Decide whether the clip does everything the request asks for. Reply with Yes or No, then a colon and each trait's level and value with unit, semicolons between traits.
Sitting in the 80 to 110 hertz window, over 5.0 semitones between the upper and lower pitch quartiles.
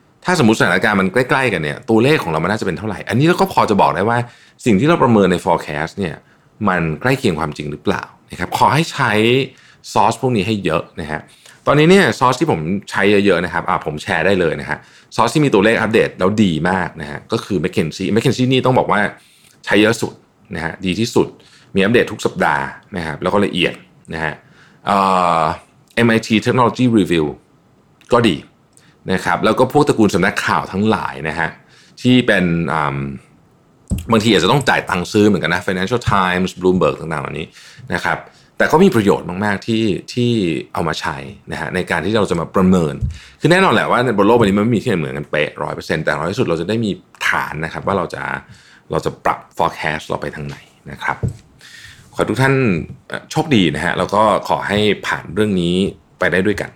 Yes: low, 100 Hz; wide, 5.6 semitones